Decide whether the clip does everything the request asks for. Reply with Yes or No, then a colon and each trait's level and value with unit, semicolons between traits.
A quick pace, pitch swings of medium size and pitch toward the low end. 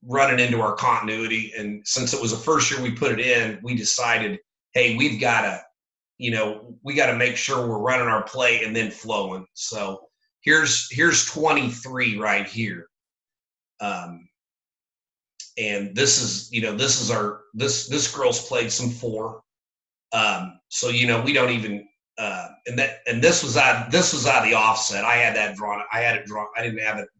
No: average, 195 wpm; average, 3.2 semitones; low, 115 Hz